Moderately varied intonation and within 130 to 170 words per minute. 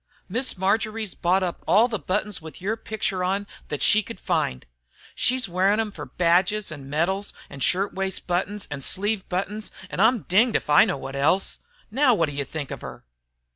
No: average, 4.4 semitones; average, 190 wpm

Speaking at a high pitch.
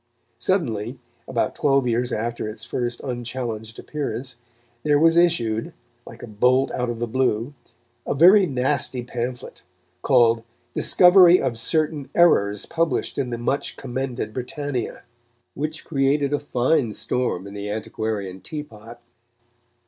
No: low, 125 Hz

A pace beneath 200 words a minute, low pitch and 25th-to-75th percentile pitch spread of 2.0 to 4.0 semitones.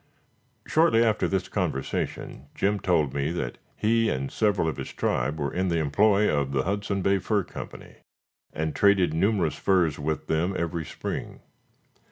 No: average, 160 wpm; very low, 90 Hz; average, 4.7 semitones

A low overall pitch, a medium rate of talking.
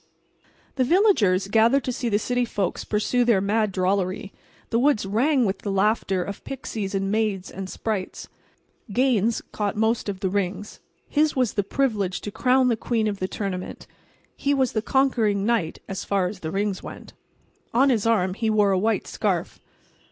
No: high, 210 Hz; average, 175 wpm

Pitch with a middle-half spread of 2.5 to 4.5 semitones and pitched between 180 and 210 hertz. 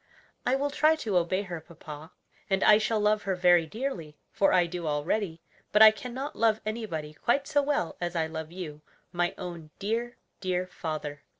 No: average, 5.1 semitones; medium, 185 Hz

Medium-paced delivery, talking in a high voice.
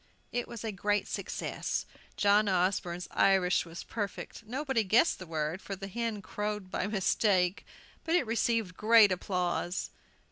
Yes: average, 145 wpm; high, 200 Hz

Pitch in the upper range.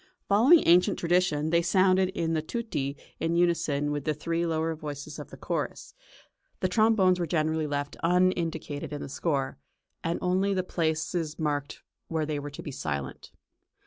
No: medium, 165 Hz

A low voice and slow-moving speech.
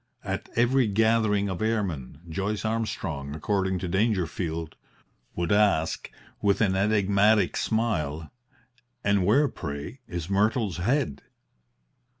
Yes: low, 100 Hz; slow, 110 wpm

